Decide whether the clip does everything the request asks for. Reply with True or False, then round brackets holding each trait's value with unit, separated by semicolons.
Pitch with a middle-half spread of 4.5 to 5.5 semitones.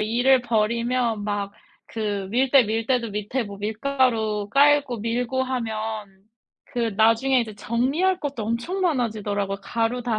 False (3.4 semitones)